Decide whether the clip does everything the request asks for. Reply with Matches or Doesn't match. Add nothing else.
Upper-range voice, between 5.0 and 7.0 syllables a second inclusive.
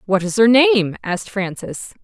Doesn't match